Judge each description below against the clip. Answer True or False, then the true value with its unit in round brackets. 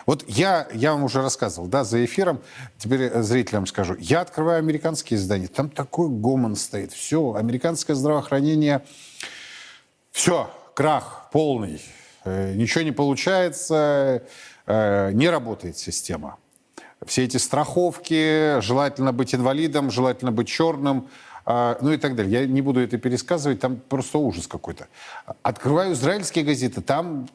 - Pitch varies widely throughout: False (4.0 semitones)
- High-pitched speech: False (135 Hz)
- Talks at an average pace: True (125 wpm)